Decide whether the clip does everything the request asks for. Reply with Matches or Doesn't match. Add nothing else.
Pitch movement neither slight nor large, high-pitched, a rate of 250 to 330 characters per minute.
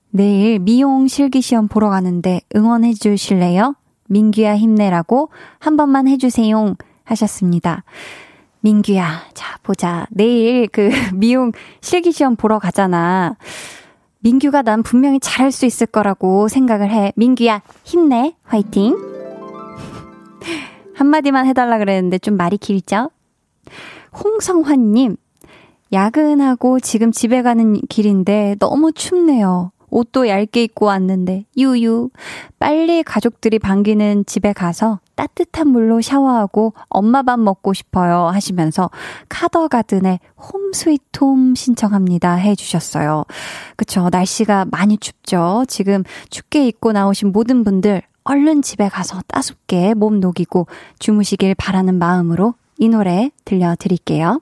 Matches